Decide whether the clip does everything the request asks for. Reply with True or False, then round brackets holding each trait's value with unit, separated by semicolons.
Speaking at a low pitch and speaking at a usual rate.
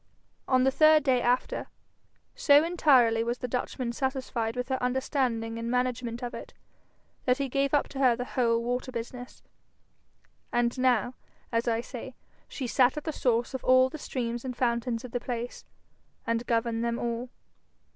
False (250 Hz; 170 wpm)